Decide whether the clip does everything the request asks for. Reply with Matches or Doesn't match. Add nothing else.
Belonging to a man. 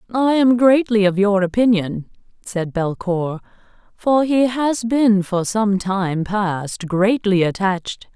Doesn't match